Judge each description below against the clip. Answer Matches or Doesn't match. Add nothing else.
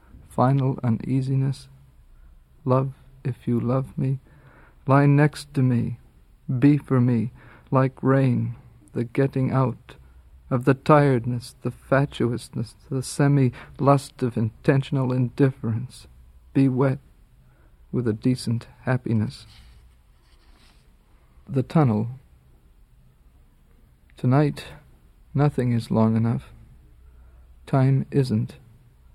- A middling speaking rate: Doesn't match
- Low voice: Matches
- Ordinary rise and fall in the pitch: Matches